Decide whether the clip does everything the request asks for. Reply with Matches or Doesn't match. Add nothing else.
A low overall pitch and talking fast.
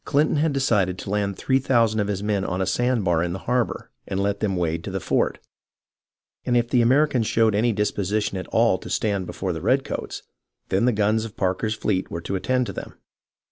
Matches